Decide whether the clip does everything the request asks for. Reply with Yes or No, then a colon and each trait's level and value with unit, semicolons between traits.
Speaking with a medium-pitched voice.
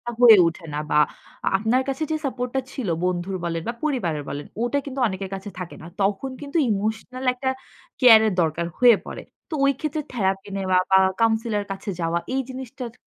No: high, 220 Hz